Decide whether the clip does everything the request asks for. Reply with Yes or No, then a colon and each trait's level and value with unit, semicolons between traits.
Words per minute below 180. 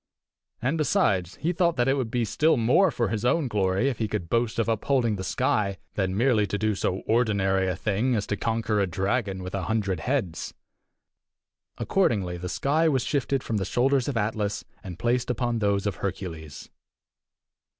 No: average, 185 wpm